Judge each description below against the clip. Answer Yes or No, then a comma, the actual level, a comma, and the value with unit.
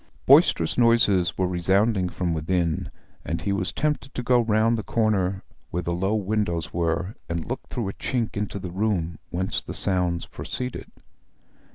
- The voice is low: Yes, very low, 95 Hz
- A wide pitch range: No, average, 4.0 semitones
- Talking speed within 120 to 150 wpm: No, average, 165 wpm